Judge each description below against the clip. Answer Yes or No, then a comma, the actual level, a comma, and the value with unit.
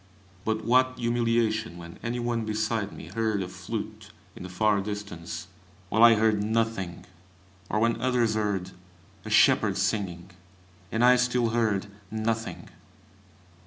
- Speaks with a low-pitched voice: Yes, low, 110 Hz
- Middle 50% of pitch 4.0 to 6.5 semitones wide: No, average, 2.8 semitones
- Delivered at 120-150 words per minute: Yes, slow, 135 wpm